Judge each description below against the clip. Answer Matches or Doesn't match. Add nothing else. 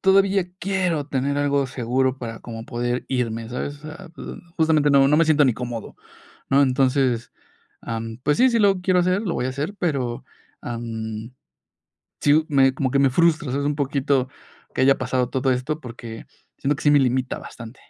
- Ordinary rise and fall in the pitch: Matches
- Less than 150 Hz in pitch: Matches